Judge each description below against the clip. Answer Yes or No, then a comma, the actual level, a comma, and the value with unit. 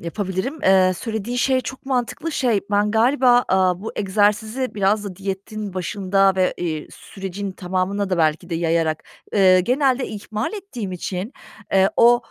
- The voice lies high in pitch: Yes, high, 200 Hz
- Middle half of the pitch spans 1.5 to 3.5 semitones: No, average, 4.2 semitones